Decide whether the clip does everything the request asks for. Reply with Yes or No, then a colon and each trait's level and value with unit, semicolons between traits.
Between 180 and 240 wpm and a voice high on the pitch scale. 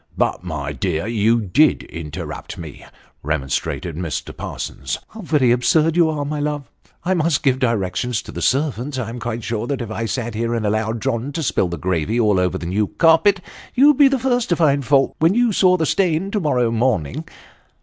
No: fast, 205 wpm; low, 125 Hz